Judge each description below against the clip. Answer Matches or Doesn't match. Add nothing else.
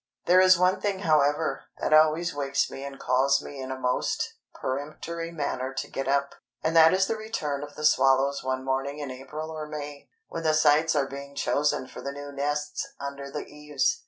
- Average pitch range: Doesn't match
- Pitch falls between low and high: Matches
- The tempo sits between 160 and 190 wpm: Doesn't match